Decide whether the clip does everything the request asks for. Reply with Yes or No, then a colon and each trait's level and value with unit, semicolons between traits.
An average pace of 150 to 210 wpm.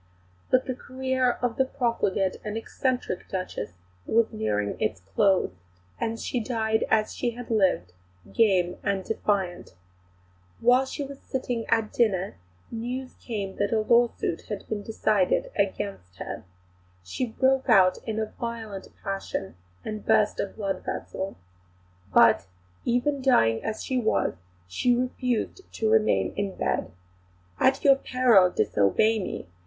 No: average, 140 wpm